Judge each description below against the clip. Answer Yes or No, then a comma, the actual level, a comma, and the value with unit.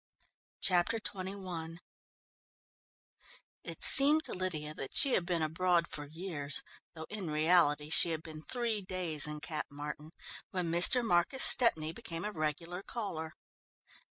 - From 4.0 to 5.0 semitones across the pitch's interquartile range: No, average, 3.6 semitones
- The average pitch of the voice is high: No, medium, 170 Hz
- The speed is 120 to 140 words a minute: Yes, slow, 135 wpm